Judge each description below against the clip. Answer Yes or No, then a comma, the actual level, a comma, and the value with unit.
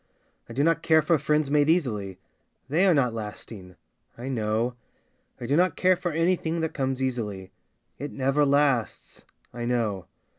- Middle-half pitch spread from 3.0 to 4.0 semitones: No, wide, 5.5 semitones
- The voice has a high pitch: No, low, 135 Hz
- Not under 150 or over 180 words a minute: Yes, average, 175 wpm